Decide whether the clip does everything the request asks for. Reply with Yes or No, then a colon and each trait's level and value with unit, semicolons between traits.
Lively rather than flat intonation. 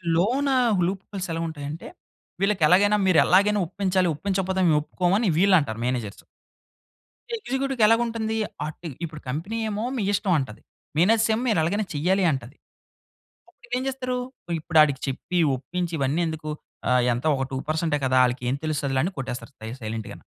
Yes: wide, 6.2 semitones